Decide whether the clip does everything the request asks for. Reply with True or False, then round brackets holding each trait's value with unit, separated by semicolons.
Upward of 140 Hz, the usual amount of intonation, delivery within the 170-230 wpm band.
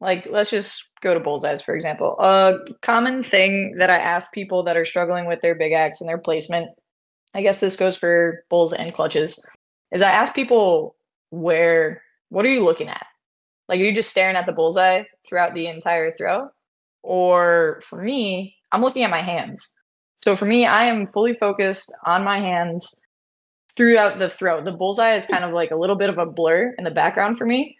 True (185 Hz; 3.5 semitones; 200 wpm)